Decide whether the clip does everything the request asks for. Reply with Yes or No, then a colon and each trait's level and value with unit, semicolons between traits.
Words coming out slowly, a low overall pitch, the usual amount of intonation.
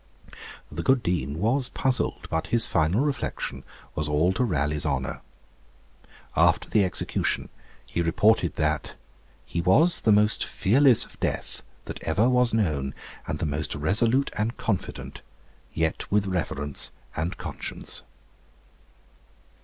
No: slow, 130 wpm; very low, 95 Hz; wide, 6.8 semitones